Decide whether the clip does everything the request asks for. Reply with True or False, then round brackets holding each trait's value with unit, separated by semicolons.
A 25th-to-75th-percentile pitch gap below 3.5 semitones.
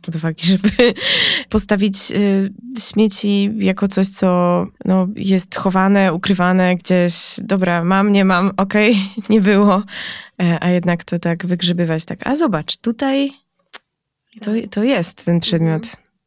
True (2.9 semitones)